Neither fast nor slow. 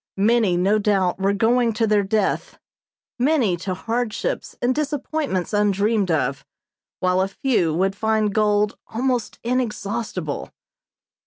No: slow, 125 wpm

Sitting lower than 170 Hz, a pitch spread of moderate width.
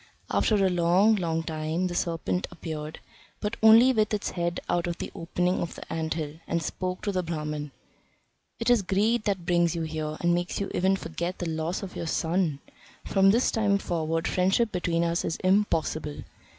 No: medium, 175 Hz; average, 3.0 semitones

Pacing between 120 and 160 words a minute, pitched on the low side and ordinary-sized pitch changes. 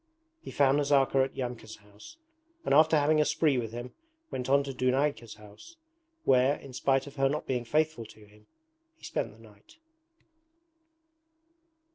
Yes: average, 155 wpm; low, 130 Hz; average, 3.9 semitones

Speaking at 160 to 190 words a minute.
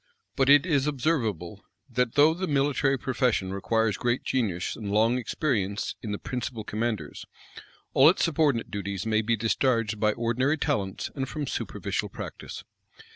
No: average, 150 wpm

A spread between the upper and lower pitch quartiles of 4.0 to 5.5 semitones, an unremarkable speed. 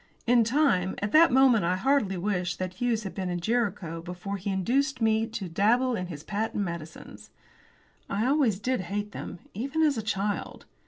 Yes: average, 4.9 semitones; average, 180 wpm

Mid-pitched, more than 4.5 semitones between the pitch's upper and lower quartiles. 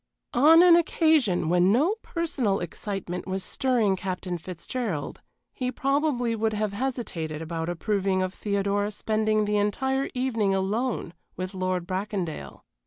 No: high, 205 Hz; average, 5.2 semitones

